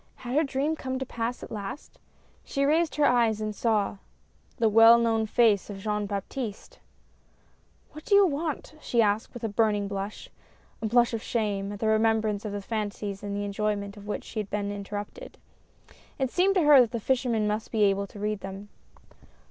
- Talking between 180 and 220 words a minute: Yes, average, 200 wpm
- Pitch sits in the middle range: No, high, 220 Hz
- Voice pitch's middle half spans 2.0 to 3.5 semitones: Yes, average, 3.2 semitones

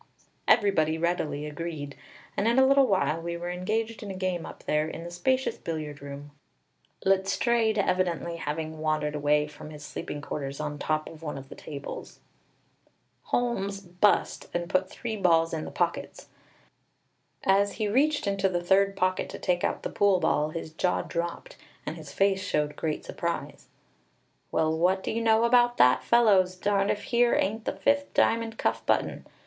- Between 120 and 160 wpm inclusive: No, average, 175 wpm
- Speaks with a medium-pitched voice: Yes, medium, 180 Hz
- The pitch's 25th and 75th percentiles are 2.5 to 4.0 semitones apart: No, average, 4.8 semitones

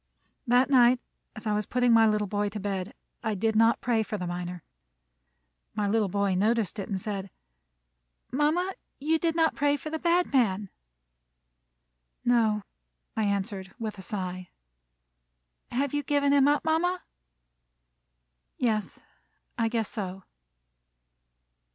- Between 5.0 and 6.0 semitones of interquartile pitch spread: Yes, wide, 5.5 semitones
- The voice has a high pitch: Yes, high, 220 Hz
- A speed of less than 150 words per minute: Yes, average, 140 wpm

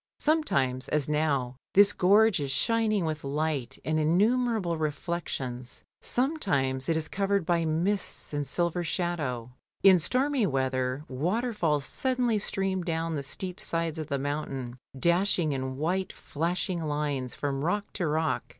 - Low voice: No, medium, 160 Hz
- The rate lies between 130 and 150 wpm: Yes, average, 140 wpm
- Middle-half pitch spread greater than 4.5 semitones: Yes, wide, 5.4 semitones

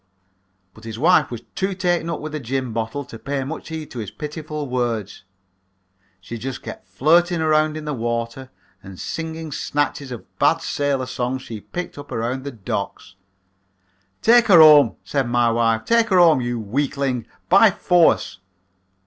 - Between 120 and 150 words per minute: No, average, 165 wpm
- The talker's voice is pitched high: No, low, 135 Hz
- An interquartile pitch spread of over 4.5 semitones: Yes, average, 5.2 semitones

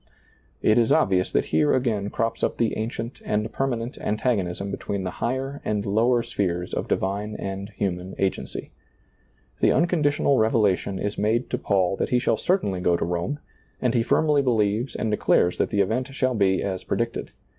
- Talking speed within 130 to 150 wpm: No, average, 175 wpm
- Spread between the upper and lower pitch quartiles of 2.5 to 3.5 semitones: No, average, 4.1 semitones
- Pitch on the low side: Yes, low, 105 Hz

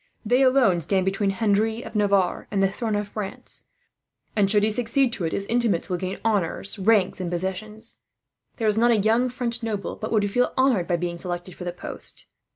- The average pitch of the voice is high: Yes, high, 205 Hz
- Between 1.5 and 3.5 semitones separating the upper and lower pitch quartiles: Yes, average, 3.2 semitones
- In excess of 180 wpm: Yes, average, 200 wpm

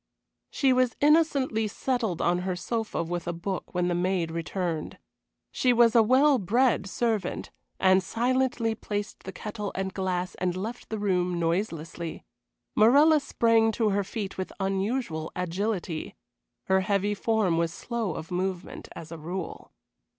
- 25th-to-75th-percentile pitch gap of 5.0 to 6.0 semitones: No, average, 4.4 semitones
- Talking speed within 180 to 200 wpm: No, average, 150 wpm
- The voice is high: Yes, high, 195 Hz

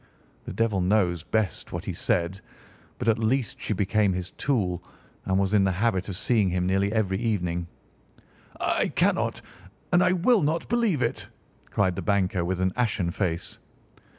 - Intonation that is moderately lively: Yes, average, 3.8 semitones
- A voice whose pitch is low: Yes, low, 100 Hz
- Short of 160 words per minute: No, average, 170 wpm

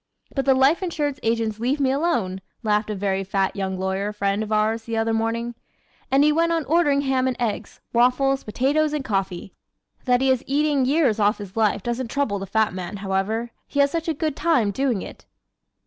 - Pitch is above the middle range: Yes, high, 235 Hz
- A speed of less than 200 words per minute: No, fast, 205 wpm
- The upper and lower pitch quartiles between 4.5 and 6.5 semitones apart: Yes, average, 5.0 semitones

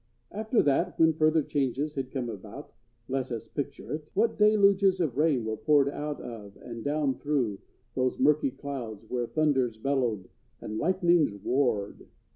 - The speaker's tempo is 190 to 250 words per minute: No, average, 145 wpm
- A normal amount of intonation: Yes, average, 4.7 semitones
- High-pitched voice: No, low, 135 Hz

